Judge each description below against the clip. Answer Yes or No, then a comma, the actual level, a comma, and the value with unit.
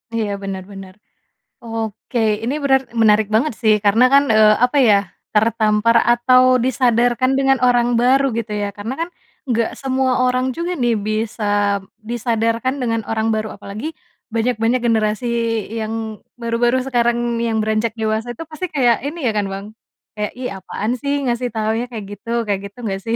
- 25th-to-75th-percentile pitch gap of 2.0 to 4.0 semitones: Yes, narrow, 2.5 semitones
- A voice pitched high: Yes, high, 230 Hz